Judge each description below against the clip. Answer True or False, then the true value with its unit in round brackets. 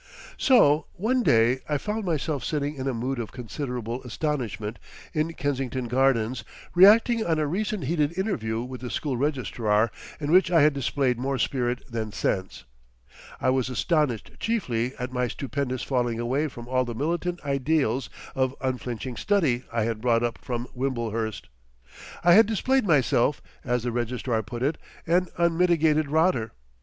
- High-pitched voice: False (130 Hz)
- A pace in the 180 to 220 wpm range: False (155 wpm)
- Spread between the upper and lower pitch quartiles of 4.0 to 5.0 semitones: True (4.7 semitones)